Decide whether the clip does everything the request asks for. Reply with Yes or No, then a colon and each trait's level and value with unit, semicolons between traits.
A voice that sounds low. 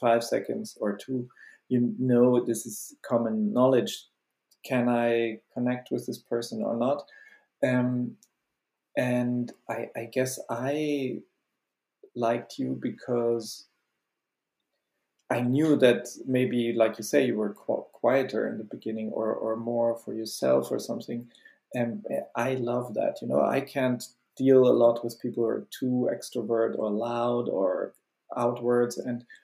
Yes: low, 120 Hz